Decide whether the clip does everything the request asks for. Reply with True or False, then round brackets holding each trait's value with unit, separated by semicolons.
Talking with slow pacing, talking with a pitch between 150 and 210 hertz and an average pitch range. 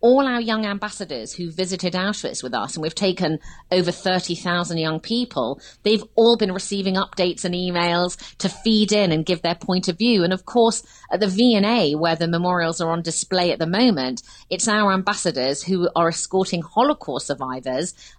False (180 wpm; 185 Hz; 3.8 semitones)